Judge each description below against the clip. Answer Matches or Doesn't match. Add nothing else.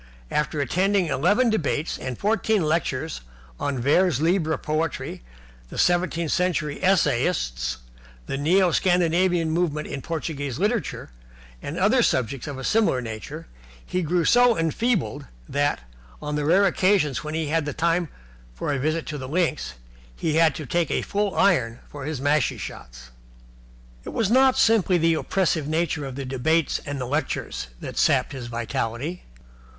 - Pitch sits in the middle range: Matches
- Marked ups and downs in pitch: Doesn't match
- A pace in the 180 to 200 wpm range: Doesn't match